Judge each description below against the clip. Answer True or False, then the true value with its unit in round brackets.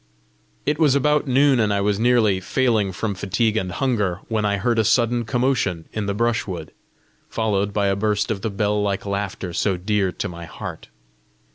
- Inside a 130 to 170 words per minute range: False (185 wpm)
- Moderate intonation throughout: True (3.1 semitones)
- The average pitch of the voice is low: True (105 Hz)